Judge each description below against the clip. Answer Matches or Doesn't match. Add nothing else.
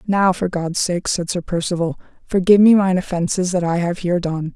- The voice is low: Doesn't match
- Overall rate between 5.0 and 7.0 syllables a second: Matches